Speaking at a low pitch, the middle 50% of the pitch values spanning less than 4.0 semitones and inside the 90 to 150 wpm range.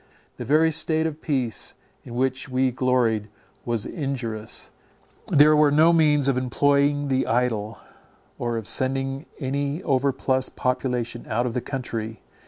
Yes: low, 130 Hz; average, 3.1 semitones; average, 145 wpm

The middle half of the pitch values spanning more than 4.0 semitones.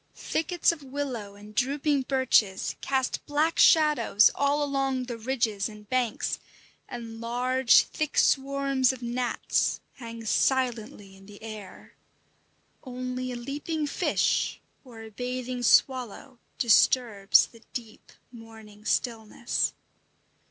No: average, 3.3 semitones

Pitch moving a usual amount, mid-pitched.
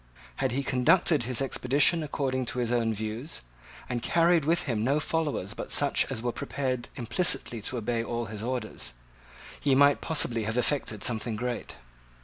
No: average, 3.6 semitones; low, 125 Hz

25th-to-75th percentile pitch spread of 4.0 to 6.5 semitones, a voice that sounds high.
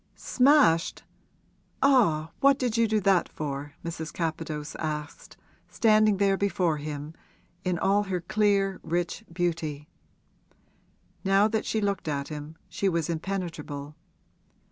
No: average, 4.7 semitones; medium, 175 Hz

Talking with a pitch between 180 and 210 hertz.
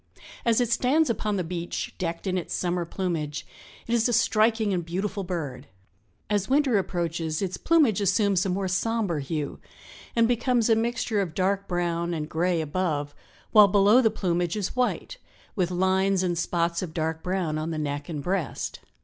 Yes: medium, 185 Hz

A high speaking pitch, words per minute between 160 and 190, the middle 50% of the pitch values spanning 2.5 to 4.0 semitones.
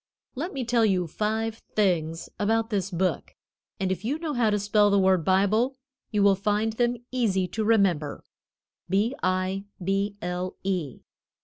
Yes: high, 200 Hz; average, 165 wpm; average, 3.1 semitones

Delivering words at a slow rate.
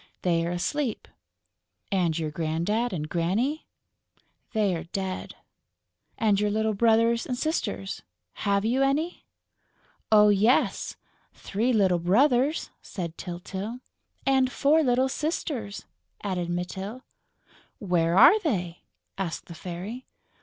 Yes: slow, 110 wpm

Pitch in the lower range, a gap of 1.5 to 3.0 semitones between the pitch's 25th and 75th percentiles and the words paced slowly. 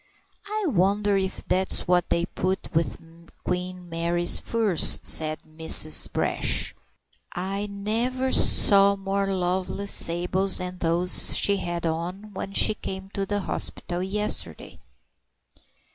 No: high, 190 Hz; narrow, 2.5 semitones; slow, 120 wpm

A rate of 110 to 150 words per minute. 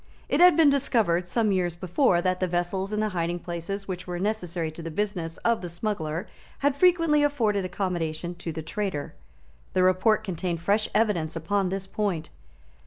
No: average, 175 wpm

